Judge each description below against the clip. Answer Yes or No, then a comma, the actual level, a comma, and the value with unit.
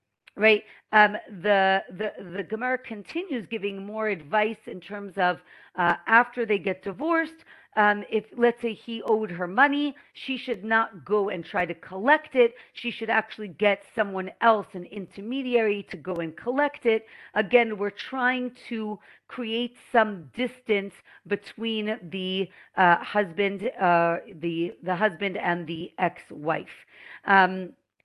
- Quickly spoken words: No, average, 145 wpm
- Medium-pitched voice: No, high, 210 Hz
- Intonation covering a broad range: No, average, 3.7 semitones